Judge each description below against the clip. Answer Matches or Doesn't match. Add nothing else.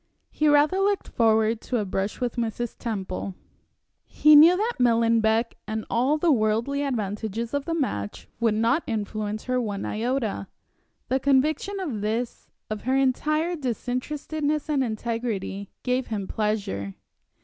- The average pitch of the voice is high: Matches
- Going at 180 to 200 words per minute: Doesn't match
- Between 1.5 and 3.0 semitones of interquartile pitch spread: Doesn't match